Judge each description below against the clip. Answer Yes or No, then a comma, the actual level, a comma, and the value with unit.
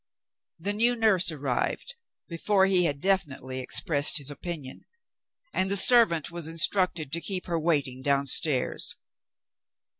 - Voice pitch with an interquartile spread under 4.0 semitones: No, average, 5.1 semitones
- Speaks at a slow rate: Yes, slow, 125 wpm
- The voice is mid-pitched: Yes, medium, 165 Hz